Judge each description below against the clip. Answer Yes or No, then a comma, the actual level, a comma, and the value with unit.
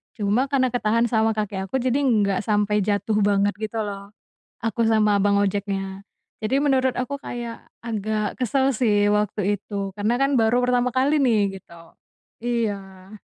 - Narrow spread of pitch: No, average, 3.3 semitones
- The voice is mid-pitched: No, high, 215 Hz